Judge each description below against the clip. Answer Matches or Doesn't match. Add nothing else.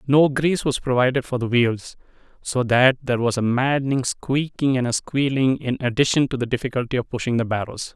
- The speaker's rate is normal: Matches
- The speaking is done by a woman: Doesn't match